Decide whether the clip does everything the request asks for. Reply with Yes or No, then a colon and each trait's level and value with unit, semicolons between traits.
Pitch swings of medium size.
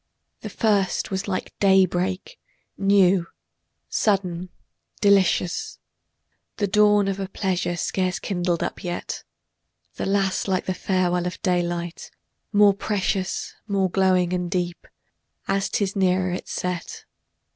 No: narrow, 1.7 semitones